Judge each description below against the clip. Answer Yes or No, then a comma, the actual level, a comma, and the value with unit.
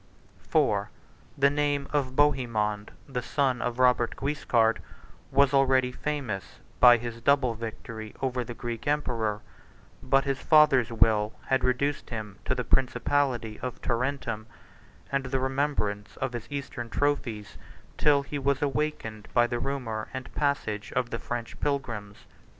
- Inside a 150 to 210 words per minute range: No, average, 140 wpm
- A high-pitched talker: No, low, 125 Hz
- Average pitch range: Yes, average, 3.4 semitones